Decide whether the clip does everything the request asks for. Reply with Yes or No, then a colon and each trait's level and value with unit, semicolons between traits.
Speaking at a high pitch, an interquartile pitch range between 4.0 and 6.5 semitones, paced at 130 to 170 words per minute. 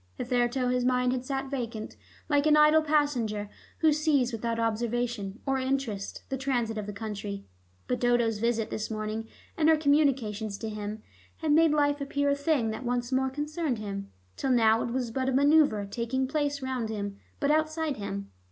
No: very high, 250 Hz; average, 4.4 semitones; average, 180 wpm